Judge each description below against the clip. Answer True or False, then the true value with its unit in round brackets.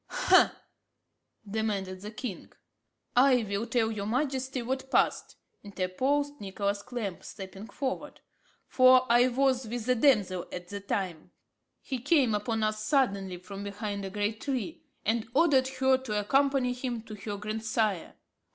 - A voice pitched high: True (225 Hz)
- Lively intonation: False (4.4 semitones)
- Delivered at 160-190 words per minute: False (140 wpm)